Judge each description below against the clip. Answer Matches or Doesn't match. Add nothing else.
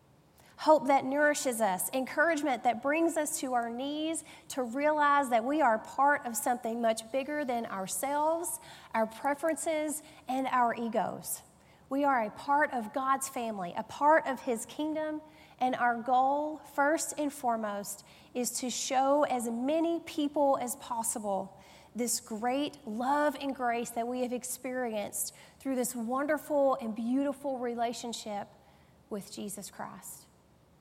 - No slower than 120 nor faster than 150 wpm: Matches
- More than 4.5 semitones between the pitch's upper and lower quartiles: Doesn't match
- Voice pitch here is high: Matches